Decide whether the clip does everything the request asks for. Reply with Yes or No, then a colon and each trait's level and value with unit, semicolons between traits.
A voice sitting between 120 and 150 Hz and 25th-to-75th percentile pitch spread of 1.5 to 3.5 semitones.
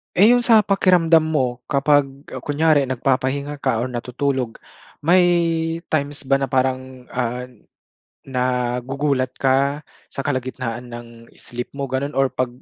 Yes: low, 135 Hz; average, 2.8 semitones